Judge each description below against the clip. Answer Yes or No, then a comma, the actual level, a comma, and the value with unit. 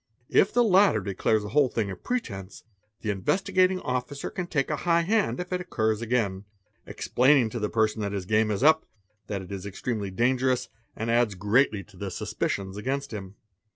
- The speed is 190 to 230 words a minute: Yes, average, 195 wpm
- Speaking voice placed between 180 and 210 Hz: No, low, 115 Hz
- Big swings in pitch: Yes, wide, 6.3 semitones